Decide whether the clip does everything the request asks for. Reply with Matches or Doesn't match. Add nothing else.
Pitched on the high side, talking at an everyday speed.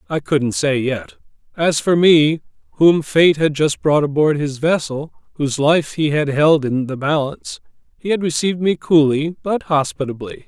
Doesn't match